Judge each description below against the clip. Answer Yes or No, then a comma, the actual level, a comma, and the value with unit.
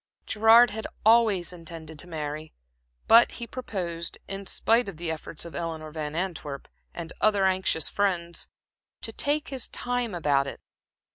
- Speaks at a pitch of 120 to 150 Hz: No, medium, 175 Hz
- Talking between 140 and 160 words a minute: Yes, average, 150 wpm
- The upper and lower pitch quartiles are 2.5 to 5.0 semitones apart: No, wide, 5.5 semitones